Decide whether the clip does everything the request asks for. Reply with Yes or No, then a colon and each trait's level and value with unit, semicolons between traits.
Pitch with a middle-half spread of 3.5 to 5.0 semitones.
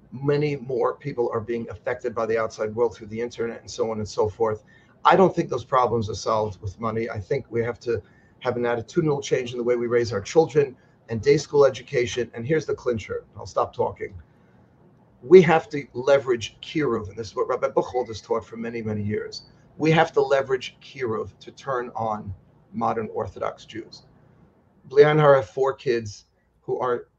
Yes: average, 4.4 semitones